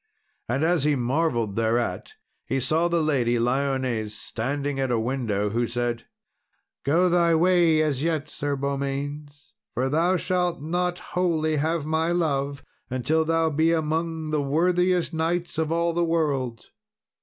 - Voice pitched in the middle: Yes, medium, 150 Hz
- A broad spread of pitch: No, average, 3.9 semitones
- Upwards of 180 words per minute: No, average, 145 wpm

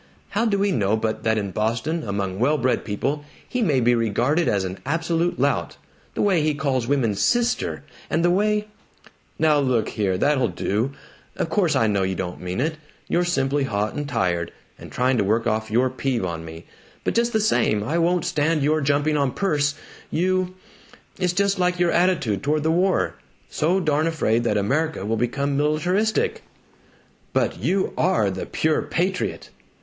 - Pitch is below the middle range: No, medium, 145 Hz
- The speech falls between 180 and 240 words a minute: Yes, average, 185 wpm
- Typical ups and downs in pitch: No, wide, 7.5 semitones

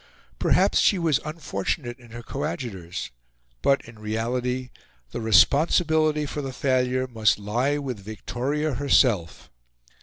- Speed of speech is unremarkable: No, slow, 120 wpm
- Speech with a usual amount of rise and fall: Yes, average, 4.4 semitones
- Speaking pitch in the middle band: No, low, 125 Hz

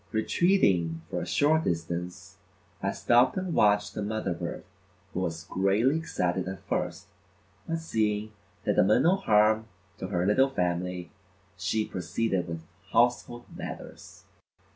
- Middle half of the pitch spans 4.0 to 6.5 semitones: Yes, average, 5.1 semitones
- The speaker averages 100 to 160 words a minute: Yes, average, 140 wpm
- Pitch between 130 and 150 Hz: No, low, 105 Hz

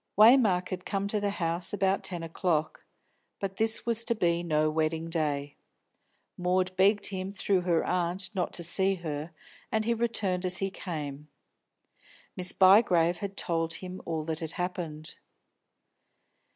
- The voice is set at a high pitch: No, medium, 180 Hz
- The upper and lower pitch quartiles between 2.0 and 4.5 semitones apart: Yes, average, 3.0 semitones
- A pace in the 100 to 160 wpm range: Yes, average, 150 wpm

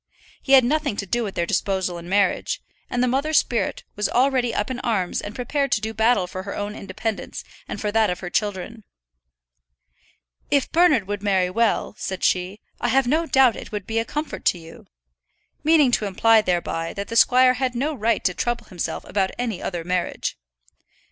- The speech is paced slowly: No, average, 195 wpm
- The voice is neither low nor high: No, high, 220 Hz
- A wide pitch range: No, average, 4.8 semitones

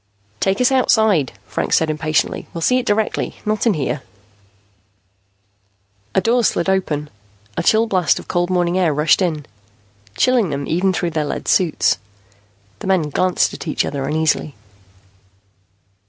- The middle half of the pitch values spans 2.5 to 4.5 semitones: No, average, 5.1 semitones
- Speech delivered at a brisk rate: No, average, 150 wpm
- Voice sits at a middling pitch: Yes, medium, 175 Hz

